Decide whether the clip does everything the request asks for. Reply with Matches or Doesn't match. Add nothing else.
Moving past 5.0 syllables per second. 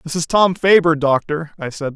Doesn't match